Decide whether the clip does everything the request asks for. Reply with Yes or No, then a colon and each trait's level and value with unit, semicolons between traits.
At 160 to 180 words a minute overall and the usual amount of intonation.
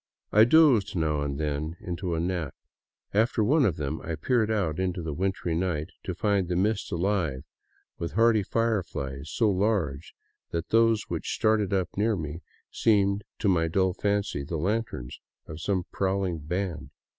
Yes: average, 165 wpm; average, 4.5 semitones